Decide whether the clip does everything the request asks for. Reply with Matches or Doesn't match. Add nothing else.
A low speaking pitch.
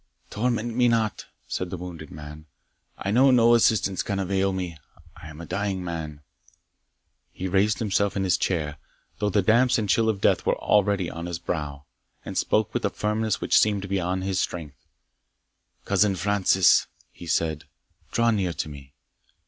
Matches